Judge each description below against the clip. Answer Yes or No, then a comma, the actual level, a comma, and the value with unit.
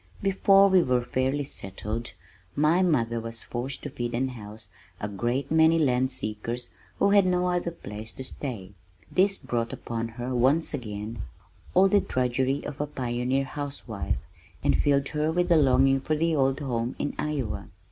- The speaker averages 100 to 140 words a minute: No, average, 165 wpm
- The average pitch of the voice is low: Yes, low, 130 Hz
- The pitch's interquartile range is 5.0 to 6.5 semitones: No, average, 4.6 semitones